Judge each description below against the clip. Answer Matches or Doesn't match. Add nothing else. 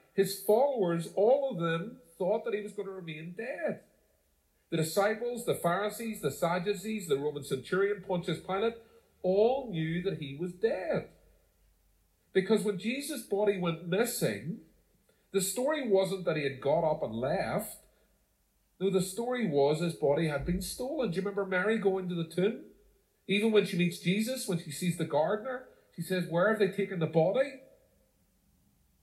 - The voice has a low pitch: Doesn't match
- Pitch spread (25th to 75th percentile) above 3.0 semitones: Matches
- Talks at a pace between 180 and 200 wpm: Doesn't match